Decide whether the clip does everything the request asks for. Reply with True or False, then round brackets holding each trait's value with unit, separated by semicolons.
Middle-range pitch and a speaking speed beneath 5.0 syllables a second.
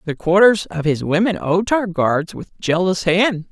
True (180 Hz; 4.3 syllables/s)